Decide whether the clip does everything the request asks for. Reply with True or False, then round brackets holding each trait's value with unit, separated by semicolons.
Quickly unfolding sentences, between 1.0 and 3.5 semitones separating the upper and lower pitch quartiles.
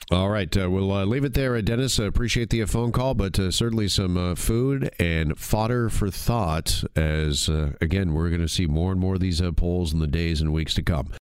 False (255 wpm; 5.2 semitones)